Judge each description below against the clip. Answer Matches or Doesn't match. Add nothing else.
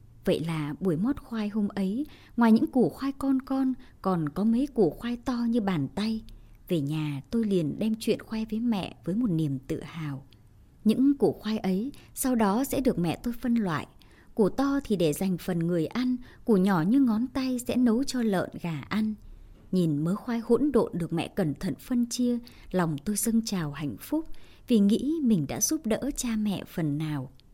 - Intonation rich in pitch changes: Matches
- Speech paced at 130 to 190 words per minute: Doesn't match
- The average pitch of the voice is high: Matches